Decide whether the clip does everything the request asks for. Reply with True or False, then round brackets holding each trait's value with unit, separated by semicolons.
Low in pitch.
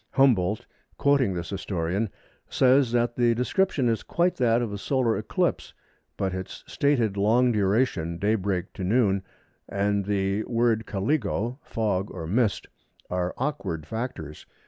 True (110 Hz)